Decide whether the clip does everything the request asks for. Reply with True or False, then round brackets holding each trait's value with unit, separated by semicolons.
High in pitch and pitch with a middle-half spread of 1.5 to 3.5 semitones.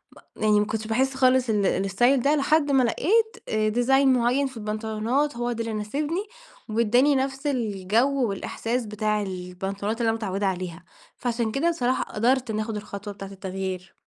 False (225 Hz; 4.1 semitones)